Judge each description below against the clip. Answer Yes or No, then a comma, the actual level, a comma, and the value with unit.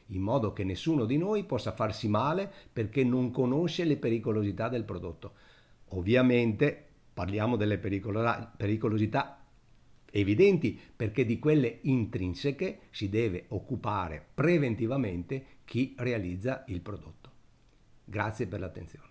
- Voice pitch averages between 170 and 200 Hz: No, low, 115 Hz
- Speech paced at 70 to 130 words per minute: Yes, slow, 115 wpm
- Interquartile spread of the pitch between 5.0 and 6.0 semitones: No, average, 4.2 semitones